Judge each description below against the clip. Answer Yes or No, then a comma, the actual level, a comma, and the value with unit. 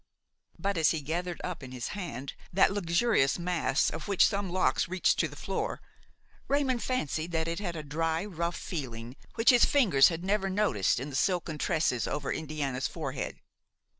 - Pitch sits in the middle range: Yes, medium, 165 Hz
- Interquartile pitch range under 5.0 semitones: No, average, 5.3 semitones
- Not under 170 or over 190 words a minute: Yes, average, 175 wpm